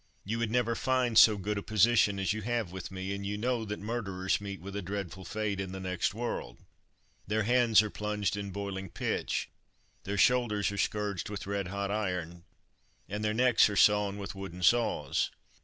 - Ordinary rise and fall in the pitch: No, narrow, 2.1 semitones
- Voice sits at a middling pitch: No, low, 100 Hz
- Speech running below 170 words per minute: No, average, 190 wpm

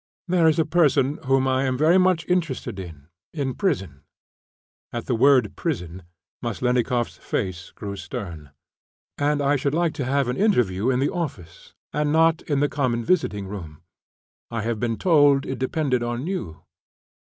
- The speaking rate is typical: Yes, average, 160 wpm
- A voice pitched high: No, low, 130 Hz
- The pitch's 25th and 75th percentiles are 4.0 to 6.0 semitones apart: Yes, wide, 5.5 semitones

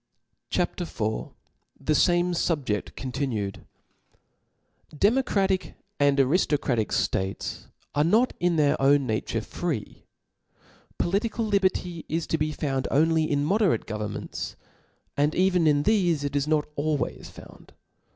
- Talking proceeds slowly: Yes, slow, 120 wpm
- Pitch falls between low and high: Yes, medium, 155 Hz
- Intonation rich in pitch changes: No, average, 4.4 semitones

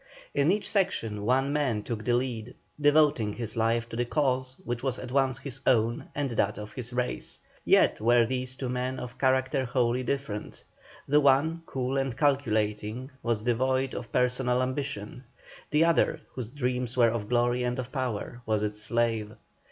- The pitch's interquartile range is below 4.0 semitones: Yes, narrow, 2.4 semitones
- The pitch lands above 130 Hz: No, low, 125 Hz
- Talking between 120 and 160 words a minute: No, average, 175 wpm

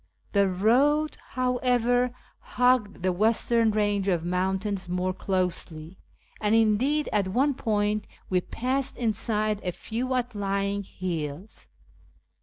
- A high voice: Yes, high, 210 Hz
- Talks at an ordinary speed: No, slow, 115 wpm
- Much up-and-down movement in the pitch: No, average, 4.5 semitones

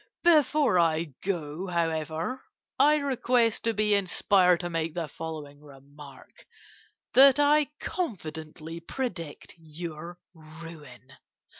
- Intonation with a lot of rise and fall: Yes, wide, 6.5 semitones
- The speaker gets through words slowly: Yes, slow, 105 wpm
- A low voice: No, medium, 170 Hz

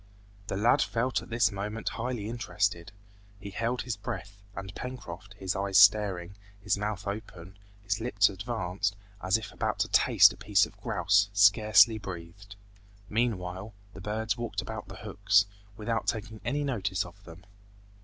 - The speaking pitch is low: Yes, low, 100 Hz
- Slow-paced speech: No, average, 155 wpm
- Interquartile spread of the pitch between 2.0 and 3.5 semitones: Yes, narrow, 2.5 semitones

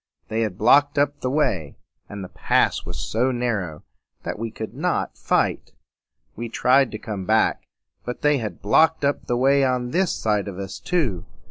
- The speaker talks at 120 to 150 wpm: No, average, 185 wpm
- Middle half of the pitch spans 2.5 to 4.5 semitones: No, average, 5.0 semitones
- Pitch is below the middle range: Yes, low, 120 Hz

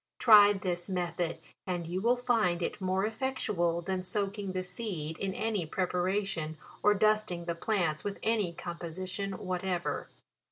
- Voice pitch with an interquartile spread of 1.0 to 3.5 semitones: Yes, average, 3.0 semitones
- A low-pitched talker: No, medium, 185 Hz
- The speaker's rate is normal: Yes, average, 155 wpm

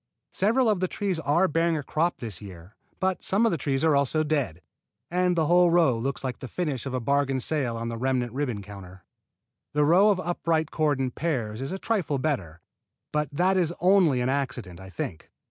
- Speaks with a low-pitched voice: No, medium, 145 Hz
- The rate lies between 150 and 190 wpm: No, fast, 205 wpm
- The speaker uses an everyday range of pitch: No, wide, 6.0 semitones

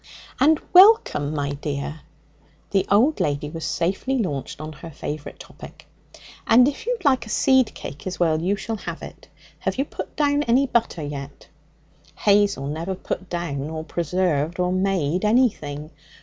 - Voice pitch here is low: No, medium, 180 Hz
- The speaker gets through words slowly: No, average, 160 wpm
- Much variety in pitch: Yes, wide, 7.8 semitones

